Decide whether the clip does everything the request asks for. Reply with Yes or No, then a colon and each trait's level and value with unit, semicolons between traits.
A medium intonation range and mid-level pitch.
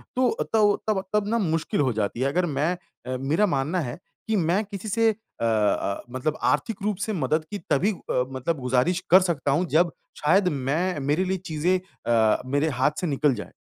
No: wide, 5.7 semitones; medium, 160 Hz